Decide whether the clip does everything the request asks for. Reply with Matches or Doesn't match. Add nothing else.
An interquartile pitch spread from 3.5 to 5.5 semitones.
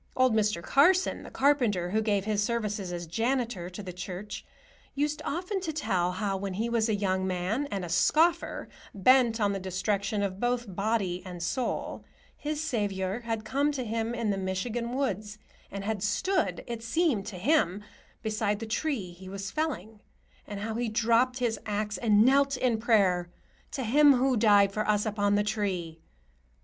Matches